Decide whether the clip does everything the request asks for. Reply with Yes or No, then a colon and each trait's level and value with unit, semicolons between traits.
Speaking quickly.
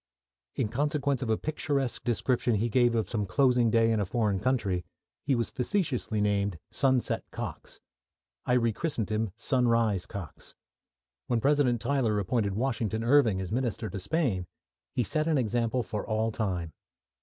No: average, 155 wpm